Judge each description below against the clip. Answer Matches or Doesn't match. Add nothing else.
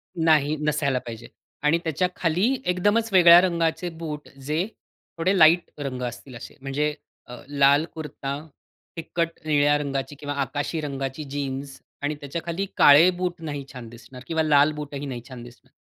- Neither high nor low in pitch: Matches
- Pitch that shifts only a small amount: Doesn't match